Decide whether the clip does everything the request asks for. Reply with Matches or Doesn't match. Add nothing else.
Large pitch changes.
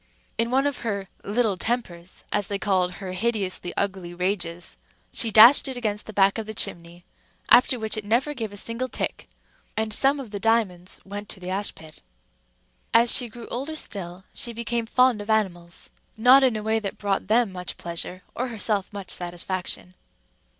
Doesn't match